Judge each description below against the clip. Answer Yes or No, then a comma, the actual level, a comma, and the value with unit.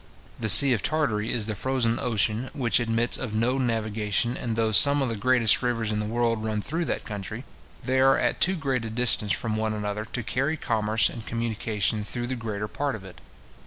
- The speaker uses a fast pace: Yes, fast, 210 wpm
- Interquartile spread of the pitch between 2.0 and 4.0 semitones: Yes, average, 2.8 semitones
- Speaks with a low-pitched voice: Yes, low, 115 Hz